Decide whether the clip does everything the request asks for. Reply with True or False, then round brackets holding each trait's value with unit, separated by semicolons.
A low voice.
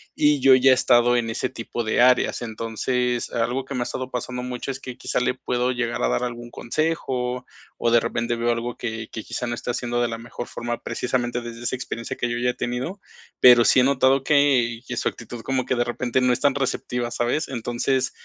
True (120 Hz)